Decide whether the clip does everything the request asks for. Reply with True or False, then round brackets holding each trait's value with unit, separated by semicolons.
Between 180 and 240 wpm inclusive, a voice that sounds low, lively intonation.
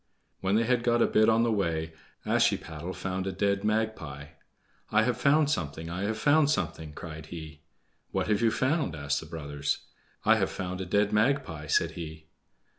True (185 wpm; 95 Hz; 5.9 semitones)